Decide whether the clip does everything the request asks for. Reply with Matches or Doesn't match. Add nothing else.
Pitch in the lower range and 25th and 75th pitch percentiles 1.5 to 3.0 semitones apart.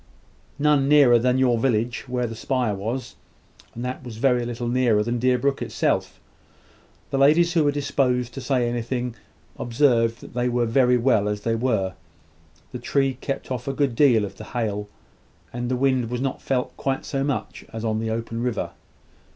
Matches